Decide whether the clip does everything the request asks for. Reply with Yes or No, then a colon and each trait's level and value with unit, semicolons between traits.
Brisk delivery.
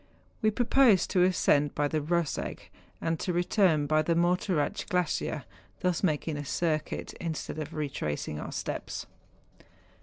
No: average, 145 wpm